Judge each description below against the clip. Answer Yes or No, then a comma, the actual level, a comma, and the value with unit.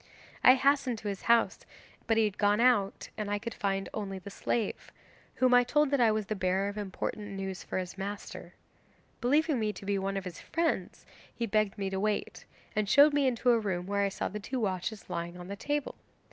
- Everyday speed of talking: No, fast, 220 wpm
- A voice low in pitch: No, high, 210 Hz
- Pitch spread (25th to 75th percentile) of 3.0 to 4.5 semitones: Yes, average, 3.8 semitones